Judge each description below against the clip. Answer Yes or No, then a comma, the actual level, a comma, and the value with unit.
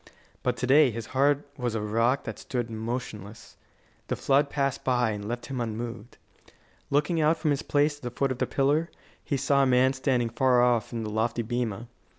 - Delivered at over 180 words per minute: Yes, average, 200 wpm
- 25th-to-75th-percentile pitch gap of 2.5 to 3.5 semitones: Yes, average, 3.1 semitones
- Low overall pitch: Yes, low, 125 Hz